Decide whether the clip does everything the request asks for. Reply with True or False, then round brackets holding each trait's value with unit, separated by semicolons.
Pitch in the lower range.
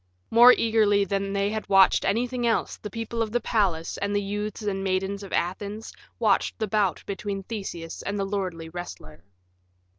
False (200 Hz)